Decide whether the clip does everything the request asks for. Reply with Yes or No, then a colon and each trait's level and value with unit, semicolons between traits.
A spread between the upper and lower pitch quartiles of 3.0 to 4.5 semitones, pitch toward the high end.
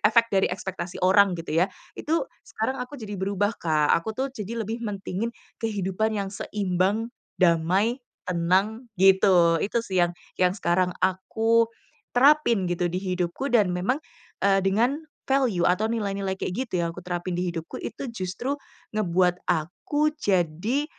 Yes: average, 4.0 semitones; high, 195 Hz